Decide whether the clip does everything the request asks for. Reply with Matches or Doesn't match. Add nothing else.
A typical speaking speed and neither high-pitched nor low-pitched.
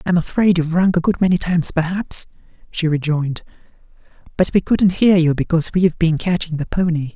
Matches